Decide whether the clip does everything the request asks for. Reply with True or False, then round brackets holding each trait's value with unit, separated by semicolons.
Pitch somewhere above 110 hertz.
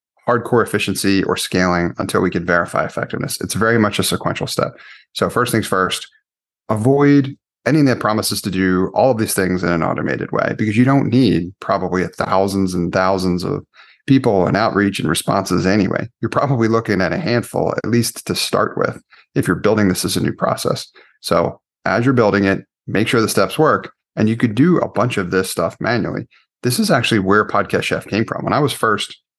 False (105 Hz)